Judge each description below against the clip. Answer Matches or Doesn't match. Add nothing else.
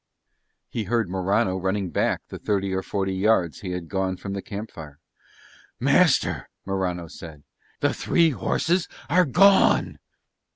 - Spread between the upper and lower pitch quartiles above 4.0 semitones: Doesn't match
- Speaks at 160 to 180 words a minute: Doesn't match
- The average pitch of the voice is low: Matches